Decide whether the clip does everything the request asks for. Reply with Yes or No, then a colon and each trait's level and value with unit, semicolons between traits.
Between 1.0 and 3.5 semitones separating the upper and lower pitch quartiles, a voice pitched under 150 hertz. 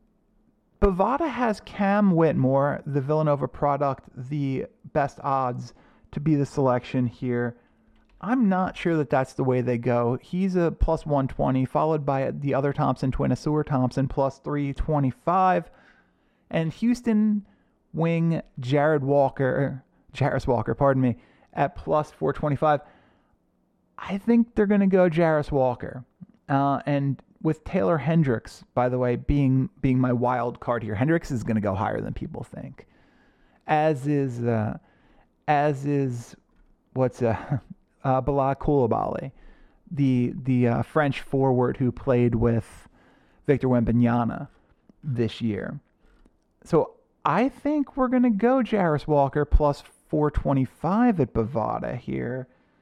No: average, 4.2 semitones; medium, 140 Hz